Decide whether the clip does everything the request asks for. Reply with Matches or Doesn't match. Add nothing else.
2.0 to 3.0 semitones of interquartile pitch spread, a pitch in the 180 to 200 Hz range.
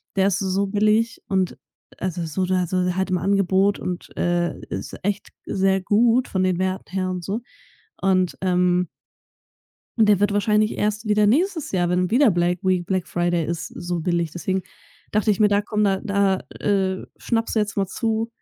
Matches